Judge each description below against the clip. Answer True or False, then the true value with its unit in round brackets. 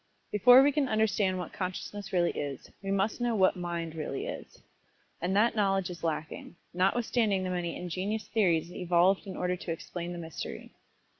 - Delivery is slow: False (175 wpm)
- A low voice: False (185 Hz)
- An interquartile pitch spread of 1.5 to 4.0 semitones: True (3.2 semitones)